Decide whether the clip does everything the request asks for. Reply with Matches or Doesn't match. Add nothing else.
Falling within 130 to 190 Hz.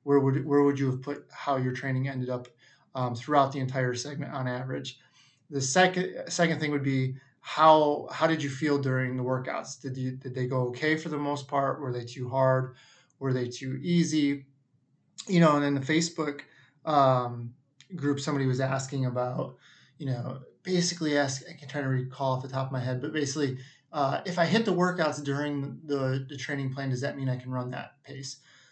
Matches